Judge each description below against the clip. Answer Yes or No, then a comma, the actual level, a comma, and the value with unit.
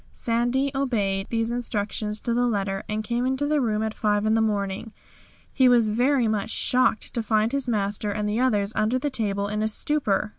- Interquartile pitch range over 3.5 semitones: No, average, 2.8 semitones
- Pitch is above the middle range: Yes, high, 220 Hz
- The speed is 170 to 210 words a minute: Yes, average, 200 wpm